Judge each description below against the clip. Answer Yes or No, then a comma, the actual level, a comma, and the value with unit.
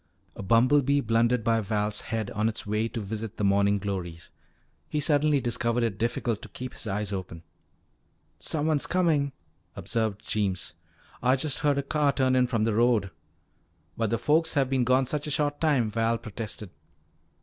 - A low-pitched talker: Yes, low, 115 Hz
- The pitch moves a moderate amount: Yes, average, 4.8 semitones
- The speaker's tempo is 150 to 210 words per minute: Yes, average, 170 wpm